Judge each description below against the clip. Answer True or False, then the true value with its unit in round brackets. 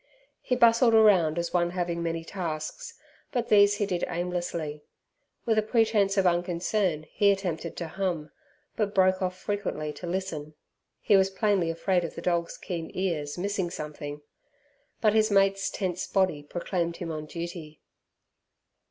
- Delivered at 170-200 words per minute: False (150 wpm)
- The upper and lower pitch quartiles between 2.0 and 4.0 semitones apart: True (3.1 semitones)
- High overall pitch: False (180 Hz)